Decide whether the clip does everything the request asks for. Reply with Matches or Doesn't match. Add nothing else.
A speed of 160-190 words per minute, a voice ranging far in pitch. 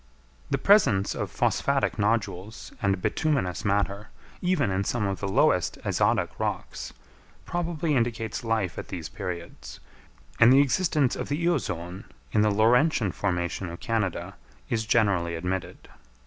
Doesn't match